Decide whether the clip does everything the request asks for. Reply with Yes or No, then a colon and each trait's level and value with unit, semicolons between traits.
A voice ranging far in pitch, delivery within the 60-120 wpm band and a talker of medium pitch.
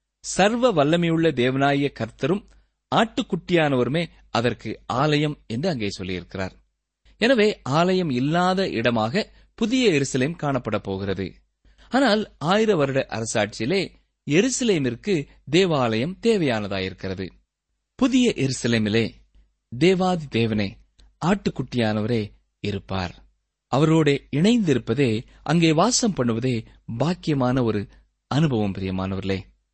No: wide, 8.3 semitones; average, 80 wpm; low, 130 Hz